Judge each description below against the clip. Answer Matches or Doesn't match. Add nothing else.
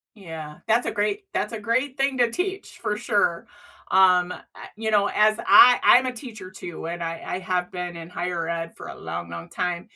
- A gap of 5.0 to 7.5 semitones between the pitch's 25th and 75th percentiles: Matches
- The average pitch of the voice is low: Doesn't match